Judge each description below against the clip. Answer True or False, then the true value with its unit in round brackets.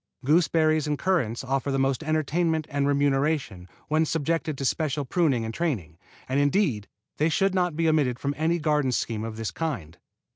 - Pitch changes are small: False (3.6 semitones)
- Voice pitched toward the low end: False (145 Hz)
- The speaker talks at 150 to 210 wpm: True (175 wpm)